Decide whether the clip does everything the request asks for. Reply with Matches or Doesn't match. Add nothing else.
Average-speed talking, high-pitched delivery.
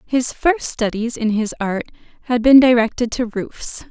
Matches